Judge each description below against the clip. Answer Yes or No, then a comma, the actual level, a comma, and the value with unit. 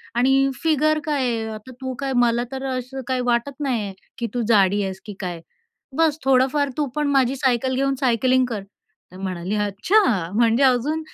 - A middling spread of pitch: Yes, average, 3.6 semitones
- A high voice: Yes, very high, 255 Hz